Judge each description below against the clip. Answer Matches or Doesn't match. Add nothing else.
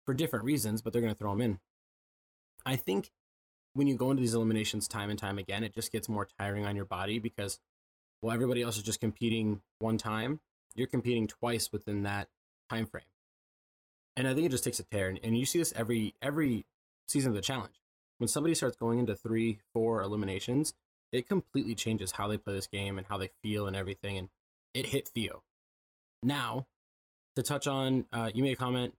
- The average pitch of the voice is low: Matches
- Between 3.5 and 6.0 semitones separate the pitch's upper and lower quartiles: Matches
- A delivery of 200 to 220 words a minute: Matches